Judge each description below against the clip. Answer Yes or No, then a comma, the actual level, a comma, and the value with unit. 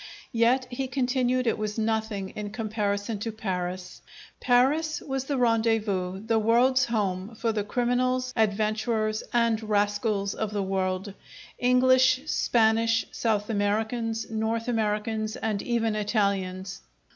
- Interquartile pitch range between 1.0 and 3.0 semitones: Yes, average, 2.7 semitones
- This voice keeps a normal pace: No, slow, 120 wpm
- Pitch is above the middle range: Yes, high, 220 Hz